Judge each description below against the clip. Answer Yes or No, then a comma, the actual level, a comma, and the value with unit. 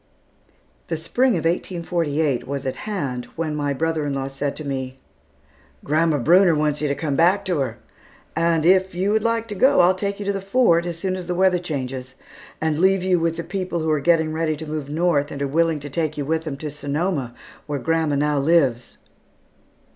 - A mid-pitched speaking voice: Yes, medium, 160 Hz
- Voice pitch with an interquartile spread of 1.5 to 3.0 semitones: No, average, 3.7 semitones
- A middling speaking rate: No, fast, 210 wpm